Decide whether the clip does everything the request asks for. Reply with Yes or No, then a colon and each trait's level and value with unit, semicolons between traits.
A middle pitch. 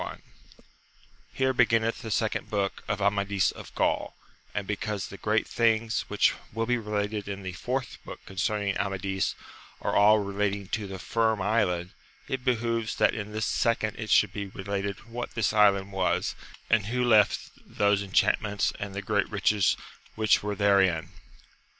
No: low, 105 Hz